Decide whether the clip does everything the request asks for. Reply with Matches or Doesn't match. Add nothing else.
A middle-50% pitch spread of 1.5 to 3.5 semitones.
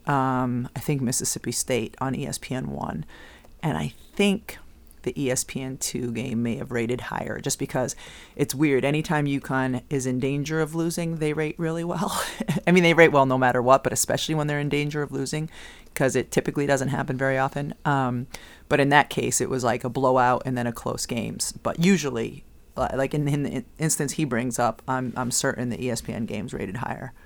Matches